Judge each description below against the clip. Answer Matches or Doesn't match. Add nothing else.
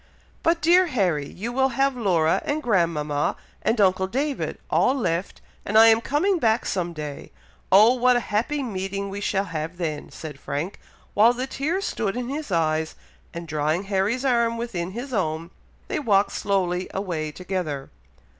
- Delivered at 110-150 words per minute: Doesn't match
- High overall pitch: Matches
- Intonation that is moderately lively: Doesn't match